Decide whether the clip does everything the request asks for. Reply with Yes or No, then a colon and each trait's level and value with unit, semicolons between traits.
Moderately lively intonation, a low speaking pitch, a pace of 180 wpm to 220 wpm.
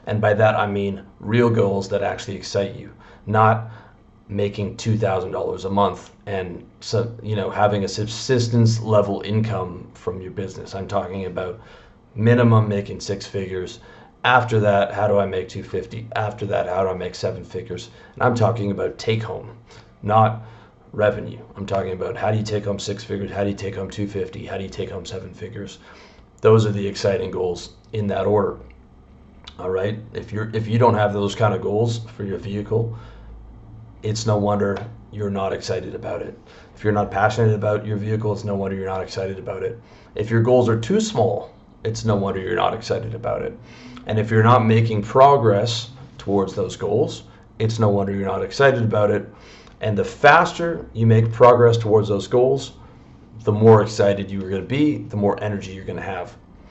No: narrow, 2.3 semitones; low, 105 Hz; average, 195 wpm